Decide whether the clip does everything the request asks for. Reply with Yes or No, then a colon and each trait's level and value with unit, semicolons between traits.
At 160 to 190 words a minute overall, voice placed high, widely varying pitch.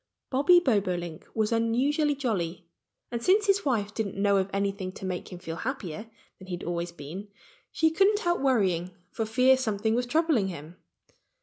Yes: average, 175 wpm; high, 215 Hz; wide, 6.3 semitones